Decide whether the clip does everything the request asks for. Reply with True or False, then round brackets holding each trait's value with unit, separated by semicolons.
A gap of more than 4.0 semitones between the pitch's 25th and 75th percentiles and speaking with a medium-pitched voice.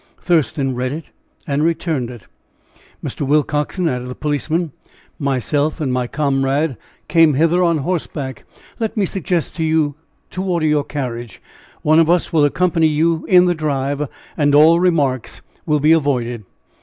False (3.3 semitones; 150 Hz)